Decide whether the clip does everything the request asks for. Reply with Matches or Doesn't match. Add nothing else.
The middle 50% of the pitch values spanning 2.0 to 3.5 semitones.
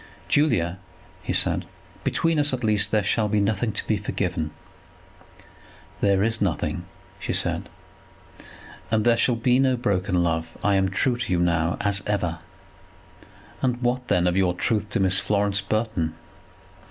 Doesn't match